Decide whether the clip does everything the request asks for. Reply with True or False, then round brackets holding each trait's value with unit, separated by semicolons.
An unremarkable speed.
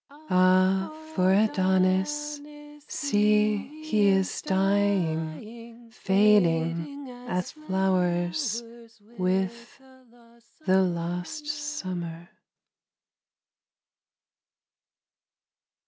False (55 wpm)